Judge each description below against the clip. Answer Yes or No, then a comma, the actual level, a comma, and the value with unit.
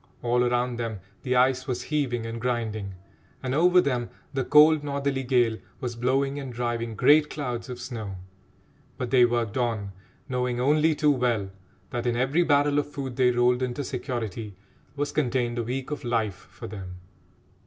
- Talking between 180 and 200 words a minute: No, average, 170 wpm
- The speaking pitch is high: No, low, 125 Hz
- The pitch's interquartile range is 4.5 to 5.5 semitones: No, average, 2.8 semitones